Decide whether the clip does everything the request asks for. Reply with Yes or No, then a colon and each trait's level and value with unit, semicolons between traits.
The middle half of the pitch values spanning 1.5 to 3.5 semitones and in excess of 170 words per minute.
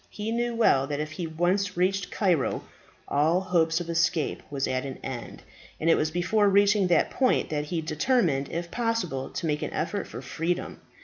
No: average, 4.3 semitones; average, 190 wpm